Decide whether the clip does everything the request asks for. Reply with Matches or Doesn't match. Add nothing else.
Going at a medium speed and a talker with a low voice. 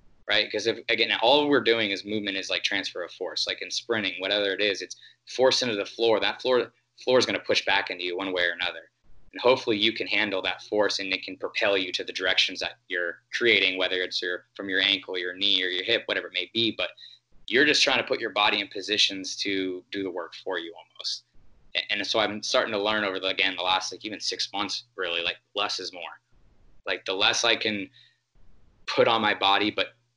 Doesn't match